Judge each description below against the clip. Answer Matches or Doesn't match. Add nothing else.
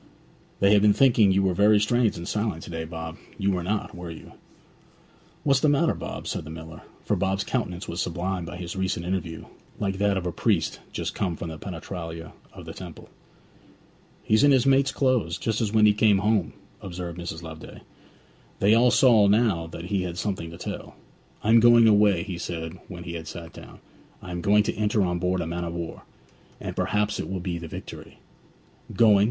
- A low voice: Matches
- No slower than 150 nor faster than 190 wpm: Doesn't match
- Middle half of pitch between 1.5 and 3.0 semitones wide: Doesn't match